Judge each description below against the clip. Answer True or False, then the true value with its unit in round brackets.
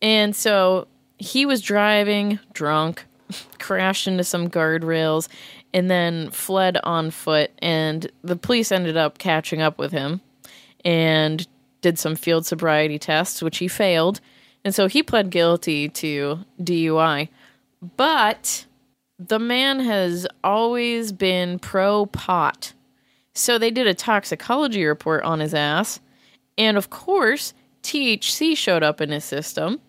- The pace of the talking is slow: True (130 wpm)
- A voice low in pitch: False (180 Hz)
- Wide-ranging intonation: False (4.6 semitones)